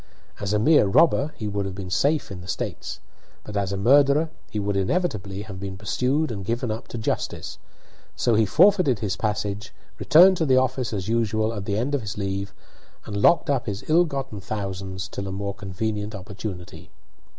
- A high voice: No, low, 105 Hz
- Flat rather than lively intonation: No, average, 4.9 semitones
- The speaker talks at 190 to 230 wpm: Yes, average, 195 wpm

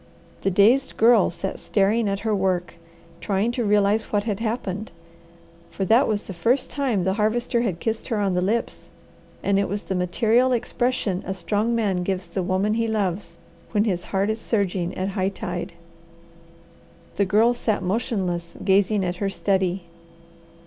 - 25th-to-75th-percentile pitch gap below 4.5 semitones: Yes, average, 2.9 semitones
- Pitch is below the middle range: No, high, 200 Hz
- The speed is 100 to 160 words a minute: No, average, 170 wpm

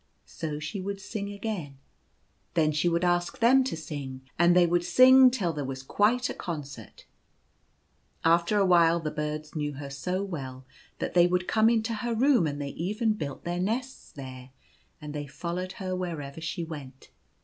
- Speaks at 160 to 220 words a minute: Yes, average, 180 wpm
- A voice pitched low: No, medium, 170 Hz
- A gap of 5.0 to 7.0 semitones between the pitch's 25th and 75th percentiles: Yes, average, 5.3 semitones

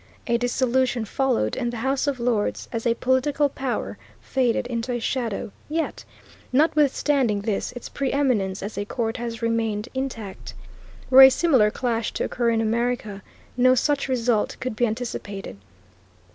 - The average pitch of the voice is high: Yes, high, 240 Hz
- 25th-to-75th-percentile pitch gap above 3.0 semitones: No, average, 2.7 semitones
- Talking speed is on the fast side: No, average, 150 wpm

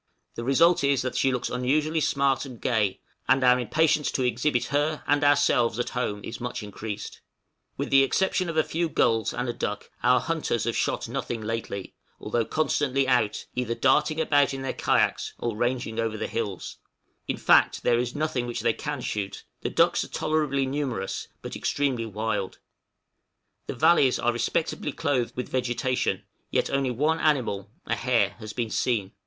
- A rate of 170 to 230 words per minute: Yes, average, 175 wpm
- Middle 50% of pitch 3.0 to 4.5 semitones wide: Yes, average, 3.8 semitones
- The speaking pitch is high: No, low, 125 Hz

